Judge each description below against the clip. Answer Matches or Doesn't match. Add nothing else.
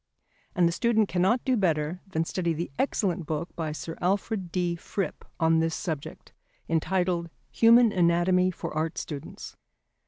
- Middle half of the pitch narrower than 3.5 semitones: Matches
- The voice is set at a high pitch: Doesn't match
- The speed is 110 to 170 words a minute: Matches